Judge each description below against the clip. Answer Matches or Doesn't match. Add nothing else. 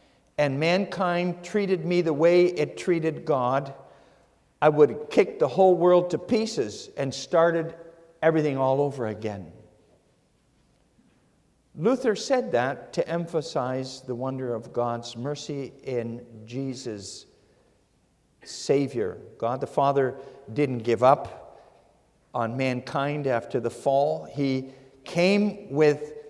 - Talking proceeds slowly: Matches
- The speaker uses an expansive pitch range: Doesn't match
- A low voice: Doesn't match